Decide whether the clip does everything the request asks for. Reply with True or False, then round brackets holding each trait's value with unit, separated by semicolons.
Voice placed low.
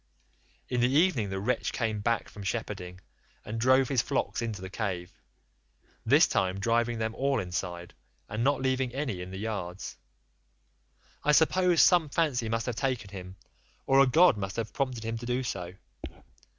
True (115 Hz)